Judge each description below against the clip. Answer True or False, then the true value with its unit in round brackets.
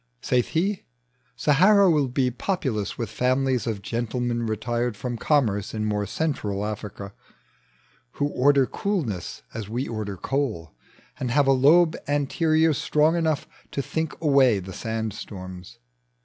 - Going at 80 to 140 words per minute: True (135 wpm)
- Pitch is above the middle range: False (125 Hz)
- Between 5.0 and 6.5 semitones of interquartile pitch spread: True (5.4 semitones)